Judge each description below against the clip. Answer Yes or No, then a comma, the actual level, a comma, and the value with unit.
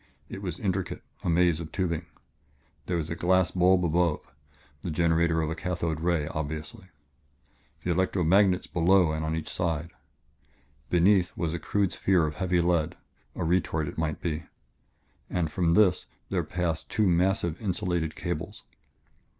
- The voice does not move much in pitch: Yes, narrow, 2.1 semitones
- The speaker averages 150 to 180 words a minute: Yes, average, 155 wpm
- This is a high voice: No, very low, 85 Hz